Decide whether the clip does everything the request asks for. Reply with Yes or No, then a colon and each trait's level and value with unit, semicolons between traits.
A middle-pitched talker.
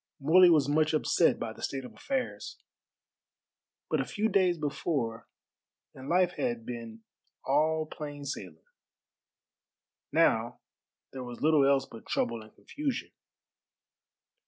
Yes: medium, 145 Hz